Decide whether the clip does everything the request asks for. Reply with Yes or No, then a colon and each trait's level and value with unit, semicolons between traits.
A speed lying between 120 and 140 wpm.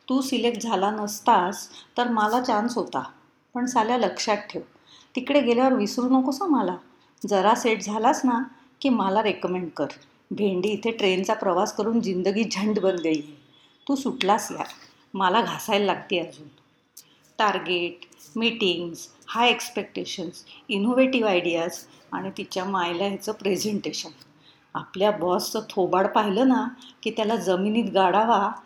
Yes: fast, 130 wpm